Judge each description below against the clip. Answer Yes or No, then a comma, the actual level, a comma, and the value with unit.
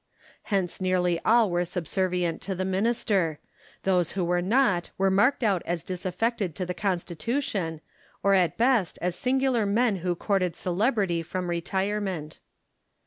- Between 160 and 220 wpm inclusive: No, average, 140 wpm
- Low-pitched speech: No, medium, 185 Hz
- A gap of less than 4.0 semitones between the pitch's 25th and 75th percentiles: Yes, average, 3.1 semitones